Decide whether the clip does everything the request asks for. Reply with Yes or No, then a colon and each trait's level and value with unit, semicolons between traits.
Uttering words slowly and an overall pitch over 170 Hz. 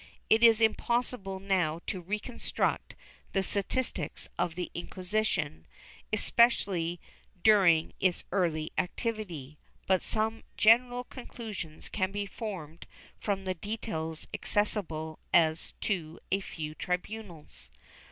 Yes: slow, 105 wpm; high, 190 Hz